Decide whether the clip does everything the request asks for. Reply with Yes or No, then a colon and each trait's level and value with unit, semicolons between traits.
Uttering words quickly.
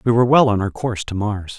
Yes: fast, 300 wpm